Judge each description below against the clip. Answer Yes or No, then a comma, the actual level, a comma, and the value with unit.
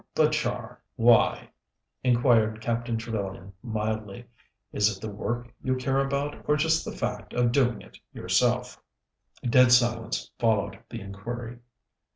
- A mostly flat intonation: Yes, narrow, 2.2 semitones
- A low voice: Yes, low, 120 Hz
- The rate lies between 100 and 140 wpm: Yes, slow, 135 wpm